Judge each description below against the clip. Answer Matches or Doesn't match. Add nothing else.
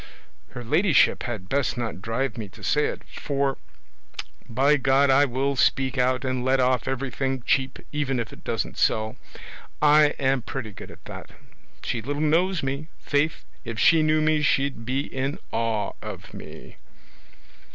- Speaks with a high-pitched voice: Doesn't match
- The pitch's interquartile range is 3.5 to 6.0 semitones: Doesn't match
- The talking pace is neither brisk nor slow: Matches